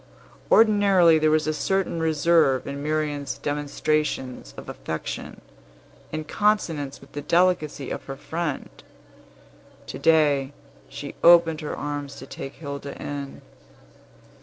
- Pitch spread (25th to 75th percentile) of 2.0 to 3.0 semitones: Yes, average, 2.7 semitones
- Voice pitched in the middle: Yes, medium, 150 Hz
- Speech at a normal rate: No, slow, 120 wpm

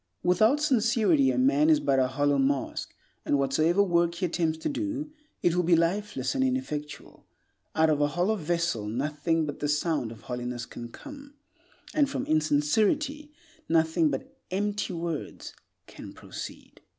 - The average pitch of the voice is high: No, medium, 170 Hz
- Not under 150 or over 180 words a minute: Yes, average, 155 wpm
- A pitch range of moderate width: No, wide, 7.8 semitones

